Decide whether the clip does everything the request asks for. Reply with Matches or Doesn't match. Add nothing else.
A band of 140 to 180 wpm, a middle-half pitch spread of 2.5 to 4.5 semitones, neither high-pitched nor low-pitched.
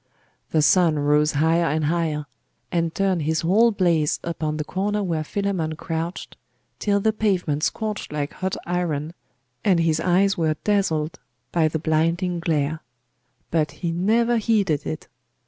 Matches